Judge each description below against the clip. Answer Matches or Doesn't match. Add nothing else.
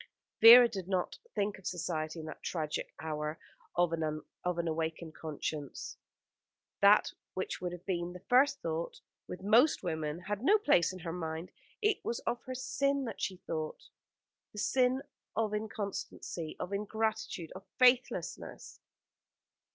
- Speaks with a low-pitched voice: Doesn't match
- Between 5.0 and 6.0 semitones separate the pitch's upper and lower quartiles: Matches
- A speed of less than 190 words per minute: Matches